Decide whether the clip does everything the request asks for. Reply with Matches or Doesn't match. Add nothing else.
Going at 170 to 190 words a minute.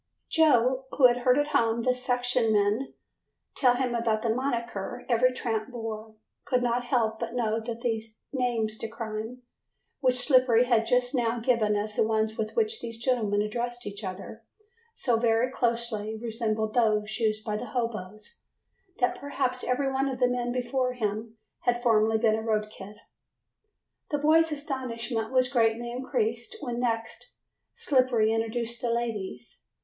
Doesn't match